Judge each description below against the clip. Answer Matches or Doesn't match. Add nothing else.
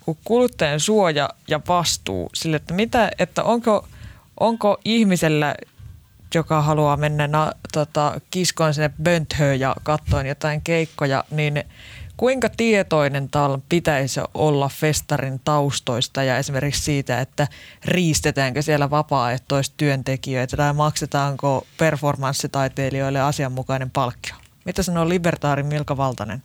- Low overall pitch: Doesn't match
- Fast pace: Doesn't match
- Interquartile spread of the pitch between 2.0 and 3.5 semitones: Matches